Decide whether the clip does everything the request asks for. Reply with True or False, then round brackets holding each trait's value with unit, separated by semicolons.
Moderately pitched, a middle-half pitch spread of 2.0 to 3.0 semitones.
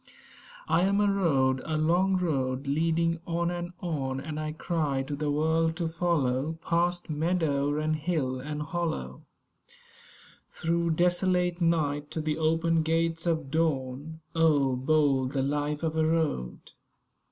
True (160 Hz; 2.7 semitones)